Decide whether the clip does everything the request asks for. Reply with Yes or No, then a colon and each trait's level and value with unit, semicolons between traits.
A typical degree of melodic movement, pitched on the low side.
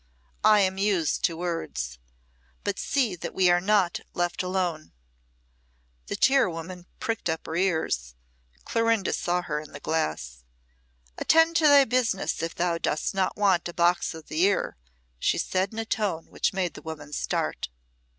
No: average, 3.9 semitones; medium, 180 Hz